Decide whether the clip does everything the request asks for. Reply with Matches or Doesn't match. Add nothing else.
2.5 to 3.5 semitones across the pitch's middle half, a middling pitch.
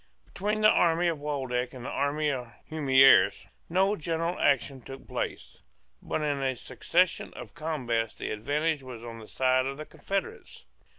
Doesn't match